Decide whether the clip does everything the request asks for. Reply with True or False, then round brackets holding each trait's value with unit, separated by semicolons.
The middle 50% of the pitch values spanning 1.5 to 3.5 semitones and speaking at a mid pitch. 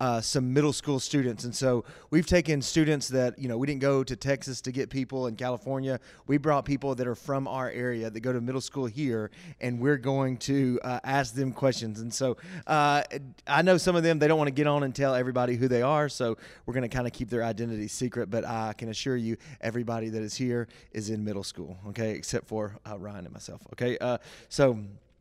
False (2.9 semitones; 125 Hz)